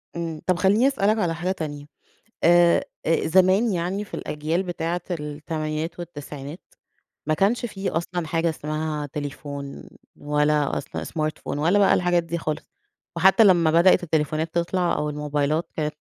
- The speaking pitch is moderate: Yes, medium, 165 Hz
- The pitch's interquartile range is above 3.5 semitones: No, average, 3.0 semitones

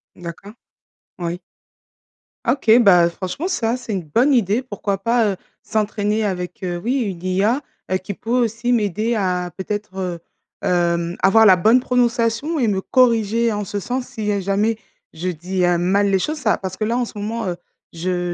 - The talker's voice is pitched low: No, high, 205 Hz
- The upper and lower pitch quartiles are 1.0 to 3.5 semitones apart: No, average, 4.1 semitones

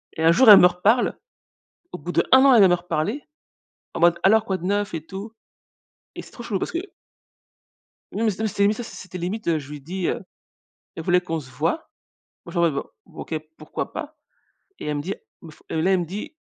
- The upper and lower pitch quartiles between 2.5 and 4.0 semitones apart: No, average, 4.4 semitones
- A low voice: No, medium, 180 Hz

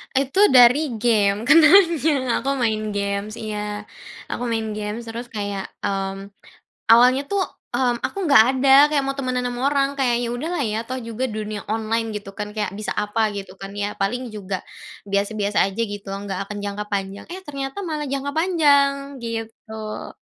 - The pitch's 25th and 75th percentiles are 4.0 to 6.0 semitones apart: Yes, average, 4.7 semitones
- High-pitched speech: Yes, high, 230 Hz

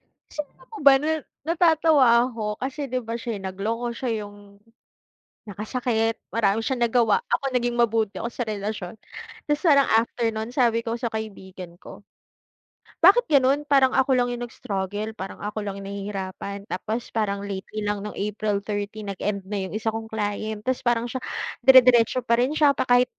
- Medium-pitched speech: No, high, 225 Hz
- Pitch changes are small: No, average, 3.7 semitones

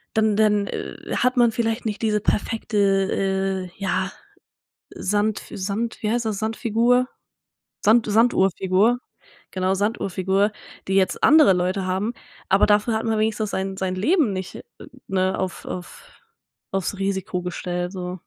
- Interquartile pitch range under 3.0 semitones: Yes, narrow, 2.6 semitones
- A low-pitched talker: No, high, 200 Hz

